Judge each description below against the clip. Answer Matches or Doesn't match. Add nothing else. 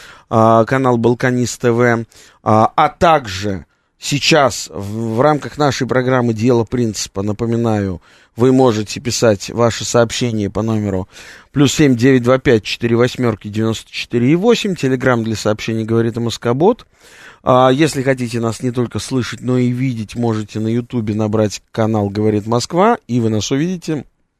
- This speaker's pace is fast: Doesn't match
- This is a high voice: Doesn't match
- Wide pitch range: Doesn't match